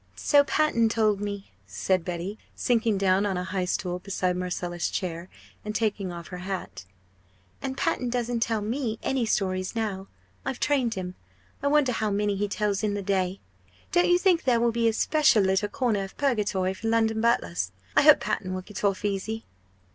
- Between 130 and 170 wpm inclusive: No, average, 185 wpm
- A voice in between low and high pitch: No, high, 205 Hz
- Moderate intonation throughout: Yes, average, 3.8 semitones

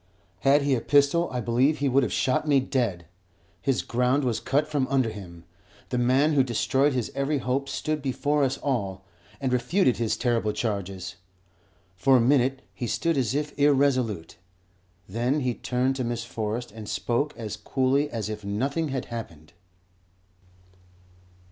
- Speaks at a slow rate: No, average, 160 wpm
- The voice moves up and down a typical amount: Yes, average, 3.4 semitones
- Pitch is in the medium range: No, low, 130 Hz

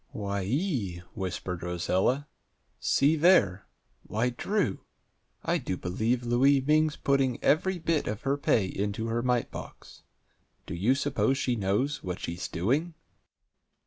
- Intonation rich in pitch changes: Yes, wide, 6.5 semitones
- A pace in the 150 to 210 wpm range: No, slow, 135 wpm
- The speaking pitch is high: No, low, 120 Hz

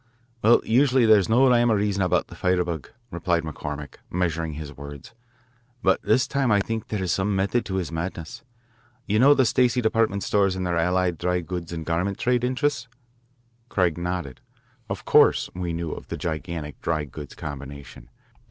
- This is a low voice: Yes, very low, 90 Hz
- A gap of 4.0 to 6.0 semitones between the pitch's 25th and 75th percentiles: Yes, average, 5.1 semitones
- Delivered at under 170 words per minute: No, average, 180 wpm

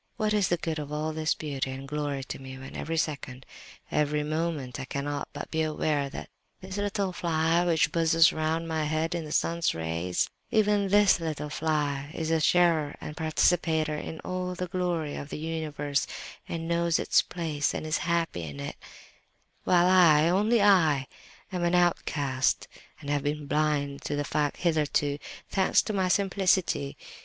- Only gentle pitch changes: No, average, 3.0 semitones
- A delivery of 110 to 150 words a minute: No, average, 165 wpm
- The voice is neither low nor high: Yes, medium, 155 Hz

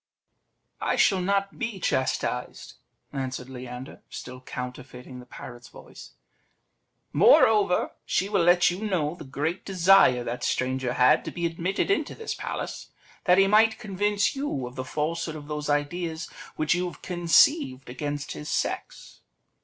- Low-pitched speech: No, medium, 160 Hz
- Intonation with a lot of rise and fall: Yes, wide, 6.8 semitones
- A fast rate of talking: No, average, 145 wpm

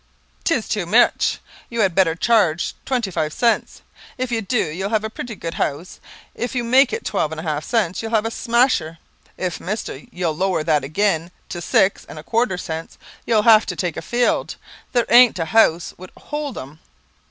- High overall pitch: Yes, high, 200 Hz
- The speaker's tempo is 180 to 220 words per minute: Yes, average, 200 wpm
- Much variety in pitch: Yes, wide, 6.0 semitones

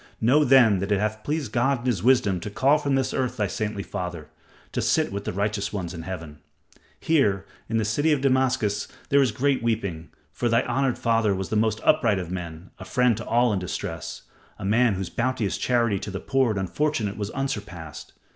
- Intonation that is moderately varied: Yes, average, 4.7 semitones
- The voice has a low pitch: Yes, low, 110 Hz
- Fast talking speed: Yes, fast, 210 wpm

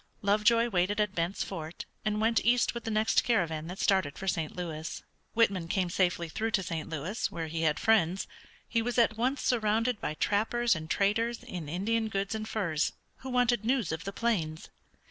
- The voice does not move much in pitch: No, average, 5.3 semitones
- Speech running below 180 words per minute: No, average, 190 wpm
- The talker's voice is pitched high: Yes, high, 200 Hz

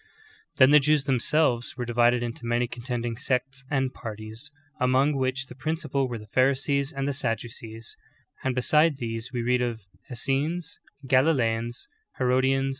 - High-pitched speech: No, low, 130 Hz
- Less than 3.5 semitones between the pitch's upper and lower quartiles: Yes, narrow, 2.5 semitones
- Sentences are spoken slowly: No, average, 150 wpm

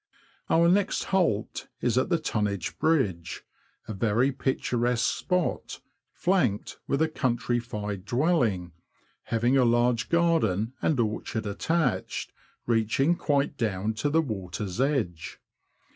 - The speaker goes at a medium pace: No, slow, 115 wpm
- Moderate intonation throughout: No, wide, 6.0 semitones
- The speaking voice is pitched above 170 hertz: No, low, 120 Hz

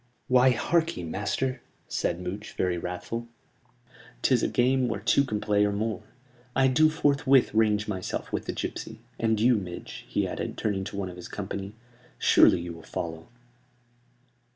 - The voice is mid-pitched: No, low, 105 Hz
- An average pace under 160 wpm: No, average, 165 wpm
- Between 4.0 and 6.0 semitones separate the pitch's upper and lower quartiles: Yes, average, 5.2 semitones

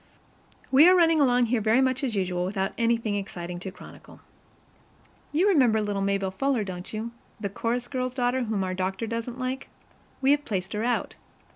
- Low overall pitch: No, high, 230 Hz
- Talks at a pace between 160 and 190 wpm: Yes, average, 180 wpm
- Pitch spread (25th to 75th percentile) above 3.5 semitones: Yes, average, 4.7 semitones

